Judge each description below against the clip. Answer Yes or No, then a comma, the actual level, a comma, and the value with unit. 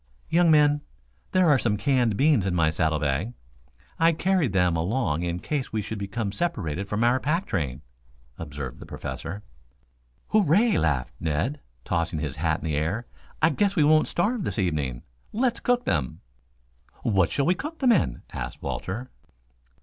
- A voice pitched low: Yes, low, 105 Hz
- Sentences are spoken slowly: No, average, 165 wpm